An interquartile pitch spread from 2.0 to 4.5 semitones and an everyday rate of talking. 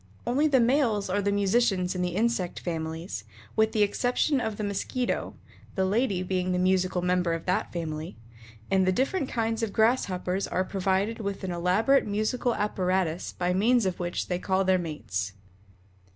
Yes: average, 3.6 semitones; average, 170 wpm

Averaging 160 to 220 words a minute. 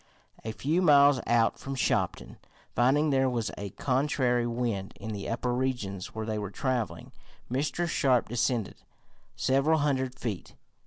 No: average, 145 wpm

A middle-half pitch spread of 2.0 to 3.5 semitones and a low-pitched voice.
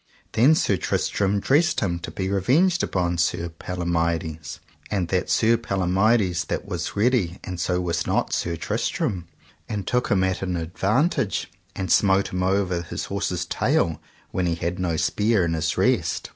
Yes: average, 3.1 semitones; very low, 90 Hz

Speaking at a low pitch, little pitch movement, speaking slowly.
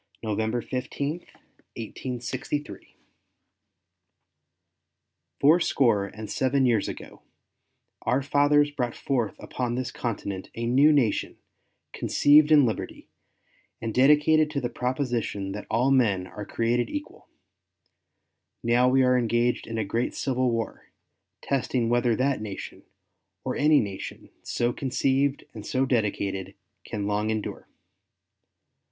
No: low, 125 Hz; average, 3.7 semitones; slow, 115 wpm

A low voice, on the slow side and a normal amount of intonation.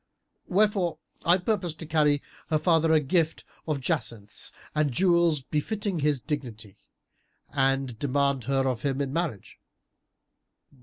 No: medium, 150 Hz; slow, 125 wpm; average, 4.1 semitones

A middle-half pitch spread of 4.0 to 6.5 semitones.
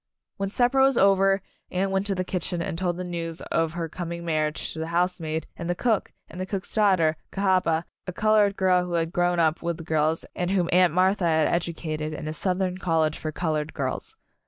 No: average, 2.7 semitones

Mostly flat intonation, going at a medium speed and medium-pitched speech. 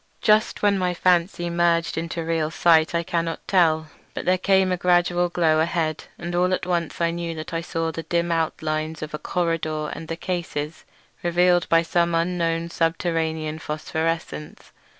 Yes: narrow, 1.6 semitones; average, 170 wpm; medium, 170 Hz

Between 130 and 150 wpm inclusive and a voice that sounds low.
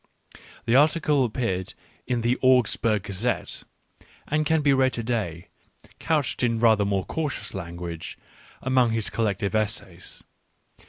Yes: average, 140 wpm; low, 115 Hz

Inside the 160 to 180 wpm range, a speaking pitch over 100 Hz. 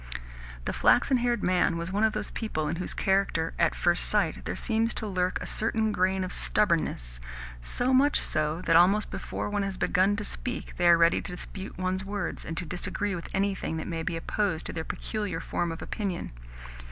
No: average, 200 wpm; medium, 185 Hz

